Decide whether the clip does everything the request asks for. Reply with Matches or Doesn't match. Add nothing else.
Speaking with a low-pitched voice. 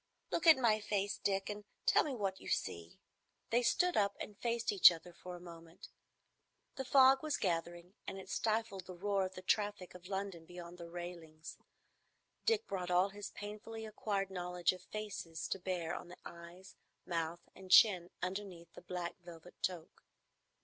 Doesn't match